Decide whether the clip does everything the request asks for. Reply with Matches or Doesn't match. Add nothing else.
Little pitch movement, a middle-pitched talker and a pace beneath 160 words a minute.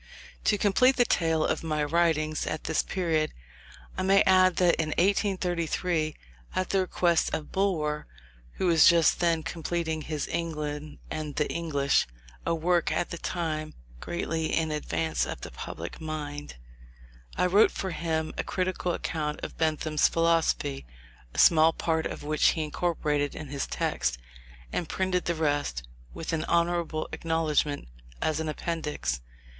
Matches